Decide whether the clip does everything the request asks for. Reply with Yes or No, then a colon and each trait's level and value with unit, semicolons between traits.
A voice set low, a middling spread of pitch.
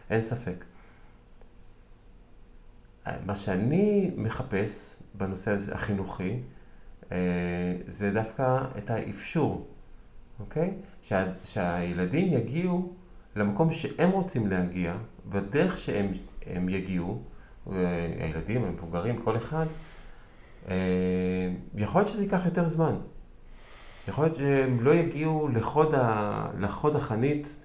No: low, 110 Hz; wide, 8.2 semitones